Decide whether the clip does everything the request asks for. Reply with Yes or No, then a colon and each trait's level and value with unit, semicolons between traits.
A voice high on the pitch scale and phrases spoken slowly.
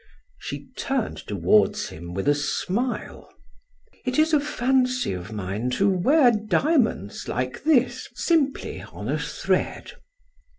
Yes: high, 215 Hz; slow, 125 wpm